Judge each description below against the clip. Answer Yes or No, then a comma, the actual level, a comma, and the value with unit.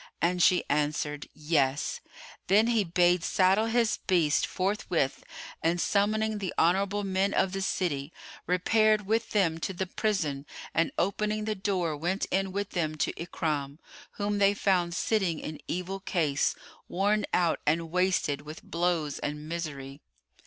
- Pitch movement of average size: Yes, average, 4.1 semitones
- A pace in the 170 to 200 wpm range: No, average, 145 wpm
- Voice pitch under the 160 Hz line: No, medium, 180 Hz